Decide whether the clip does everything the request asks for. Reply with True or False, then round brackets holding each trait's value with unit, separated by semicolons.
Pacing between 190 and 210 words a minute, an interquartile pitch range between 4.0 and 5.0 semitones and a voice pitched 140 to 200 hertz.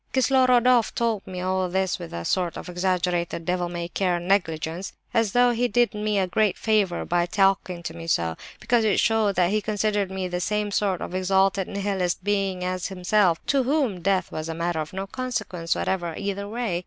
False (195 wpm; 3.1 semitones; 190 Hz)